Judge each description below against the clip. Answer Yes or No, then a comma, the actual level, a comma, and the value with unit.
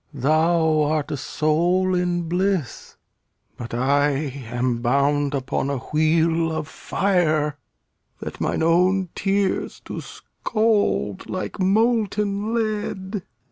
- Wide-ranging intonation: No, average, 4.9 semitones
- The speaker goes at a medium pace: No, slow, 105 wpm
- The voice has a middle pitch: Yes, medium, 165 Hz